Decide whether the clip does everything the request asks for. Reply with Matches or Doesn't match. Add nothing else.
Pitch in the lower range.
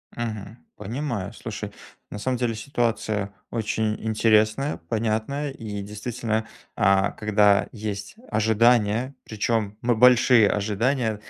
Matches